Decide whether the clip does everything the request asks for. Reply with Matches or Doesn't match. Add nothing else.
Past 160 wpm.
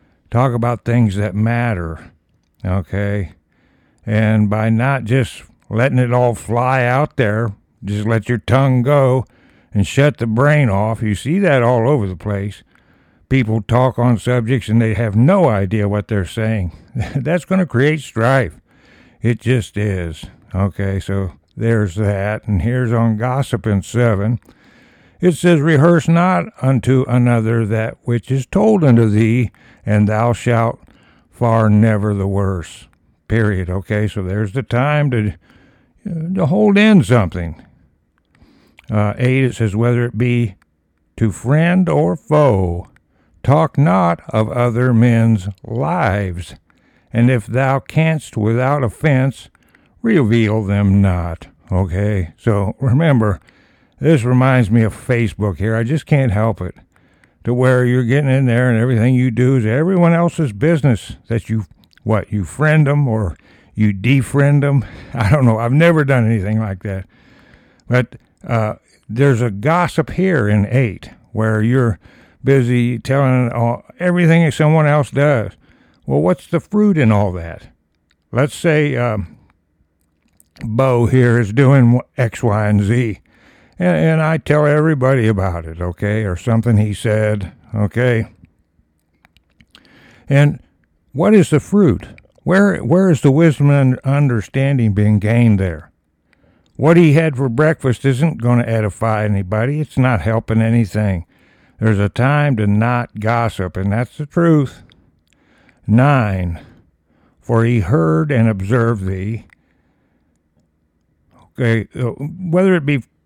Doesn't match